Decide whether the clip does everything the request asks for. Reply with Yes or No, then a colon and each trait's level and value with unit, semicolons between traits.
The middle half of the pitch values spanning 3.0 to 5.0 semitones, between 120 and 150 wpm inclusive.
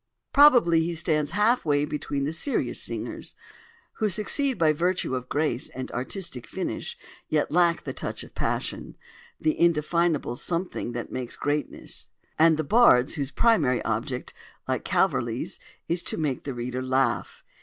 No: wide, 5.4 semitones; average, 145 wpm